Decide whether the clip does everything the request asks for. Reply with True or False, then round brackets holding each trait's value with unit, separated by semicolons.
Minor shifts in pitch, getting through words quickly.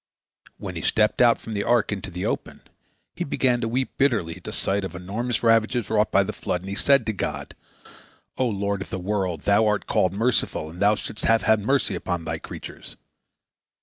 False (3.1 semitones; 215 wpm)